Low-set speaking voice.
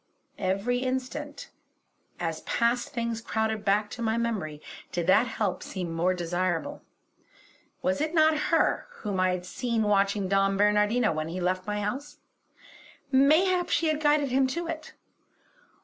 No: high, 220 Hz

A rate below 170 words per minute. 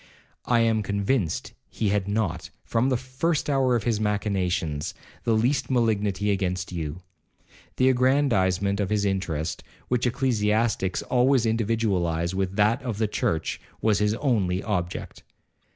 Yes: slow, 135 wpm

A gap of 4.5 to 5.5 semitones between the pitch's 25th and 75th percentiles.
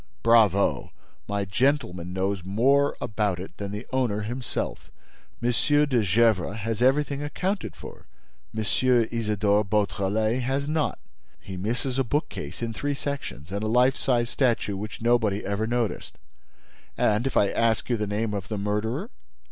No: average, 3.8 semitones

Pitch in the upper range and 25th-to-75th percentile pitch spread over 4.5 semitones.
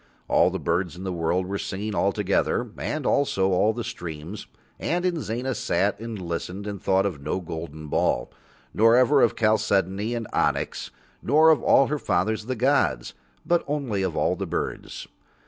No: low, 105 Hz; average, 4.9 semitones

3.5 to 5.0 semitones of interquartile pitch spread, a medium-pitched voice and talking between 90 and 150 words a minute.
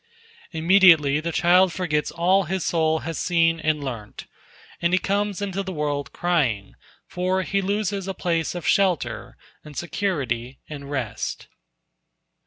Yes: average, 4.0 semitones; medium, 170 Hz; average, 140 wpm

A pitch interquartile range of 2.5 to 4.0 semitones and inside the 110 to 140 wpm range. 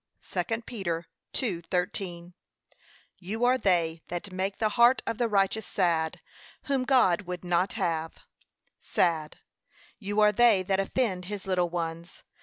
Yes: average, 3.6 semitones; slow, 135 wpm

